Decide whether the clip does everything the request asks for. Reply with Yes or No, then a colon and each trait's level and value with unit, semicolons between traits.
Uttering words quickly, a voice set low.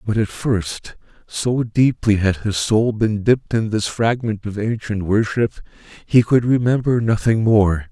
No: average, 160 wpm; low, 110 Hz